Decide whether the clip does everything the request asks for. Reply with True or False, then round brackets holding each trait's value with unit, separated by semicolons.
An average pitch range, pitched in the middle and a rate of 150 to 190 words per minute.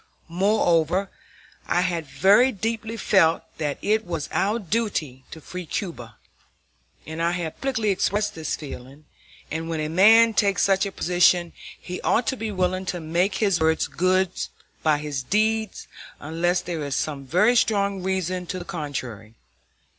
True (4.1 semitones; 180 Hz; 155 wpm)